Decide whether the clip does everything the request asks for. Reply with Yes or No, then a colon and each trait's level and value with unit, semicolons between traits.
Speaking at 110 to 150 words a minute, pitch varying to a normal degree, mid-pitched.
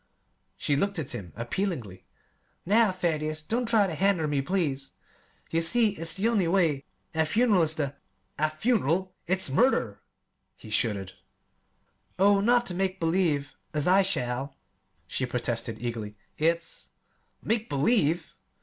No: average, 145 wpm; wide, 6.2 semitones; medium, 165 Hz